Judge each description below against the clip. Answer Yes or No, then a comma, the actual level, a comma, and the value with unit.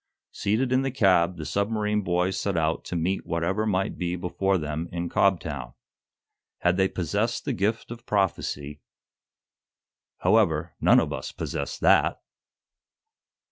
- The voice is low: Yes, very low, 95 Hz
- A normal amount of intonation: Yes, average, 3.9 semitones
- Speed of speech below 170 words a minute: Yes, average, 140 wpm